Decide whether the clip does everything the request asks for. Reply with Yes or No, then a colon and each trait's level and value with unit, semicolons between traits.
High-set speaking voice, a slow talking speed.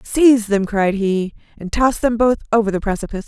No: high, 215 Hz; average, 200 wpm